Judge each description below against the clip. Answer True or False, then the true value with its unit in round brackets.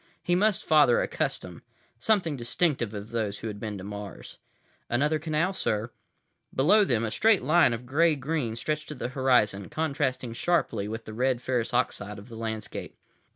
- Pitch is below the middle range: True (125 Hz)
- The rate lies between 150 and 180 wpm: True (175 wpm)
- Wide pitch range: True (5.7 semitones)